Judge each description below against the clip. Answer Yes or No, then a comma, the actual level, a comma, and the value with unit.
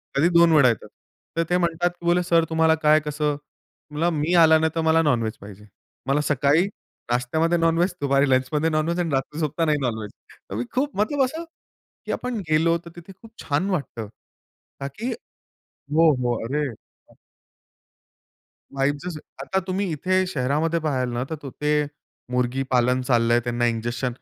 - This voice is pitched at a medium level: Yes, medium, 150 Hz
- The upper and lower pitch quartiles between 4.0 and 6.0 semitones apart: Yes, average, 4.6 semitones